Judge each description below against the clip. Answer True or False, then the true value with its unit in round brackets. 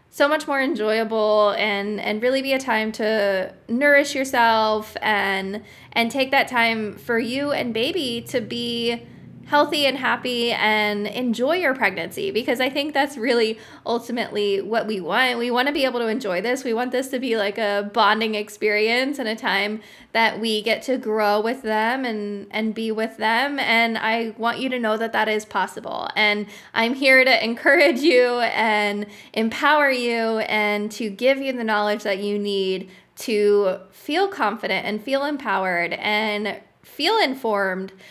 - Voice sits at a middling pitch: False (225 Hz)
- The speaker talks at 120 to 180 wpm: True (170 wpm)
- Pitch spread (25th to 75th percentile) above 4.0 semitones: False (3.3 semitones)